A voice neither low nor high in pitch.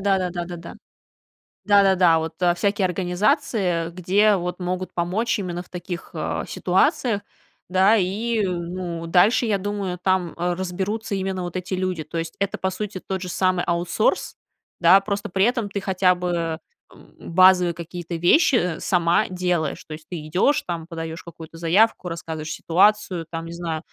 Yes: medium, 180 Hz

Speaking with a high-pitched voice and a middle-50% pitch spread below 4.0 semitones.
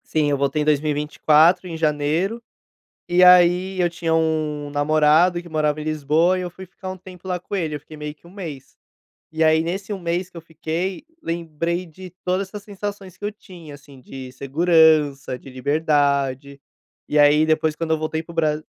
No: medium, 160 Hz; average, 3.1 semitones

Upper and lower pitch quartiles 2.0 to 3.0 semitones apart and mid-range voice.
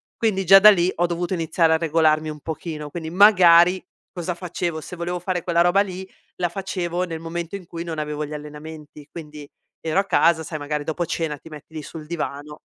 Yes: narrow, 2.4 semitones; medium, 170 Hz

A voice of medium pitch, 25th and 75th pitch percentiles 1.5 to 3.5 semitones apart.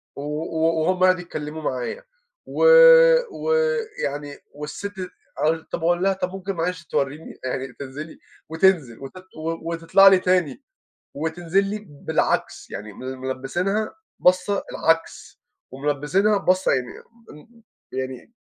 No: medium, 165 Hz; average, 4.6 semitones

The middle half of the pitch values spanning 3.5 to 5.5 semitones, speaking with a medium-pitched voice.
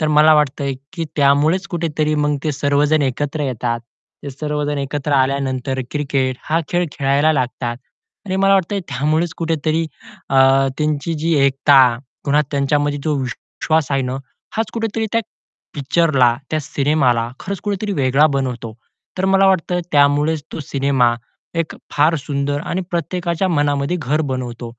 No: average, 2.9 semitones; medium, 145 Hz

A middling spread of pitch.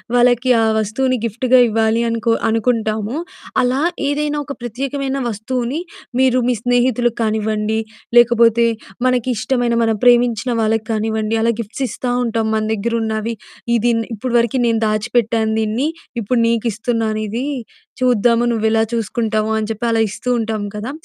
No: narrow, 2.0 semitones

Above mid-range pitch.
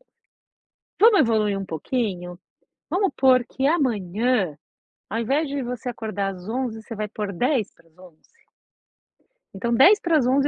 Yes: high, 235 Hz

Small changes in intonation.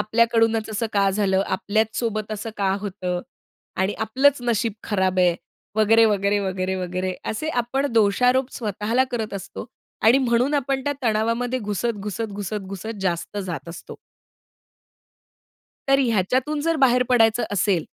No: average, 3.5 semitones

